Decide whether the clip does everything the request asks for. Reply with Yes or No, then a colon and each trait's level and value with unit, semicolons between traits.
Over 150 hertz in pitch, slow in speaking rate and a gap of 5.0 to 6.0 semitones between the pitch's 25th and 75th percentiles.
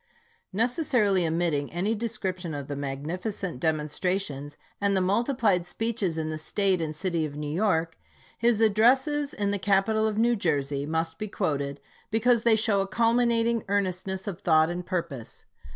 No: high, 190 Hz; average, 160 wpm; wide, 5.4 semitones